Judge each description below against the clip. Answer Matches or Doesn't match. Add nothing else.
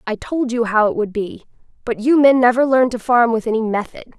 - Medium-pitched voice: Doesn't match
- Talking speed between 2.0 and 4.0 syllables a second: Doesn't match